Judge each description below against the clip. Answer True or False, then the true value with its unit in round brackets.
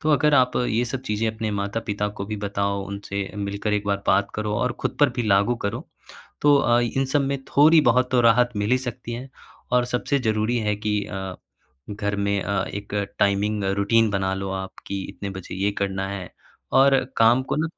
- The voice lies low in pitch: True (105 Hz)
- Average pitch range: True (3.5 semitones)